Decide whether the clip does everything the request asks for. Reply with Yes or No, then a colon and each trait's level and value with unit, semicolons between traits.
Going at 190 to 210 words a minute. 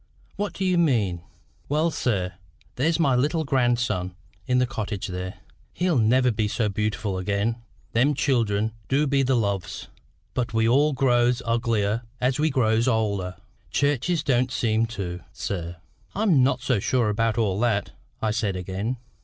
No: average, 155 wpm